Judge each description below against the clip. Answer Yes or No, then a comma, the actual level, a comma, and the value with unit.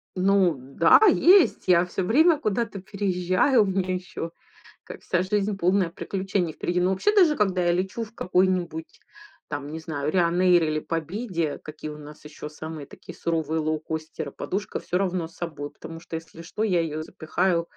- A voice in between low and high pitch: Yes, medium, 175 Hz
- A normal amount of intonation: Yes, average, 3.3 semitones